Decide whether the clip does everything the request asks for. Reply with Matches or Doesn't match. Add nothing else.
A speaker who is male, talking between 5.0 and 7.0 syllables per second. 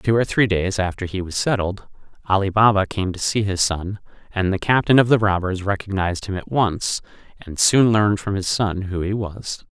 Matches